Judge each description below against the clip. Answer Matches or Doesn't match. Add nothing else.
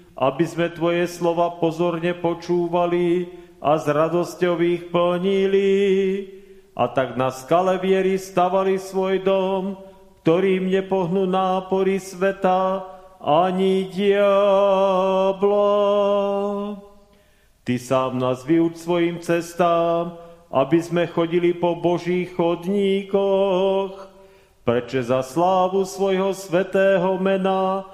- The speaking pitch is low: Doesn't match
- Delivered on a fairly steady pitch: Matches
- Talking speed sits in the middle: Doesn't match